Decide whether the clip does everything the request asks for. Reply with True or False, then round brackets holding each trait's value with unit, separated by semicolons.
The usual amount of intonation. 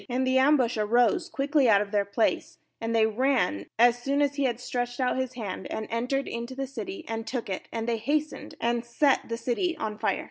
True (3.2 semitones)